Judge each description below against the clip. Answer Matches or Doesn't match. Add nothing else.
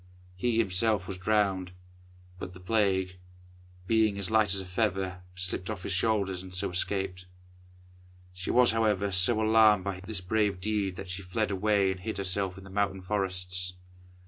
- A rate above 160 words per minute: Matches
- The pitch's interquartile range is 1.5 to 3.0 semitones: Matches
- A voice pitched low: Matches